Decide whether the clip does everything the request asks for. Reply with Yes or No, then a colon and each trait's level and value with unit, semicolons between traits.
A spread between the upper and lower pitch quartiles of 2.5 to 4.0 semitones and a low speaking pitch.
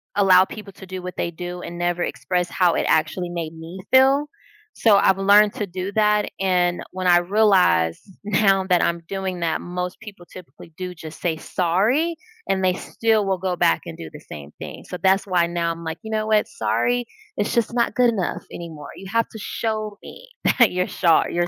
No: average, 3.2 semitones; medium, 185 Hz